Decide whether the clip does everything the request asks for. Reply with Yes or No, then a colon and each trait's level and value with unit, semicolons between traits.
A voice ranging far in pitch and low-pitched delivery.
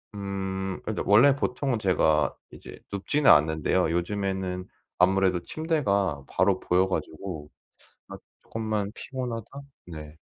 No: average, 3.3 semitones; very low, 95 Hz